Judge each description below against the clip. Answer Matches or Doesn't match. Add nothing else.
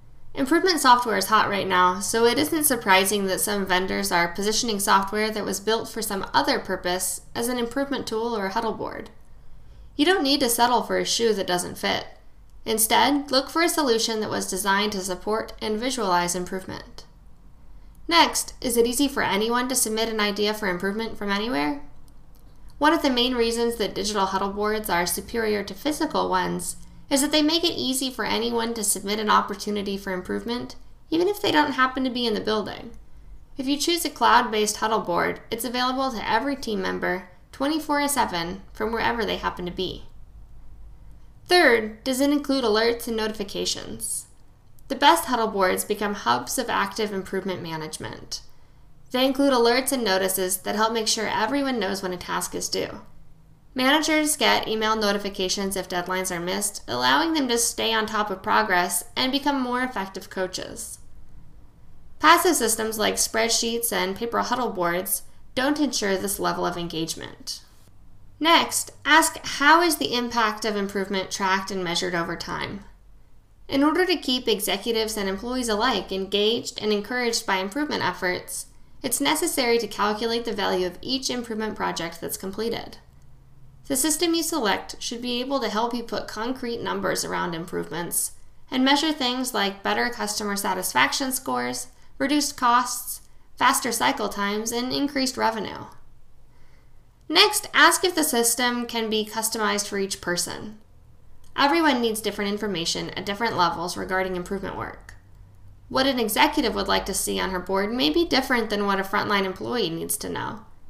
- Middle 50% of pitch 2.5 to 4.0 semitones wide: Doesn't match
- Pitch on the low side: Doesn't match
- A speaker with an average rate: Matches